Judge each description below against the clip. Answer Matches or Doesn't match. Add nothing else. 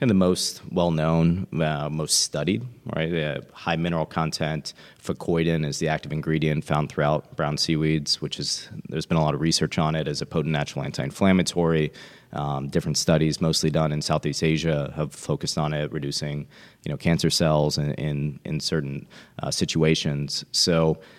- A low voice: Matches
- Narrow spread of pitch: Matches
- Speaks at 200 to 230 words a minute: Doesn't match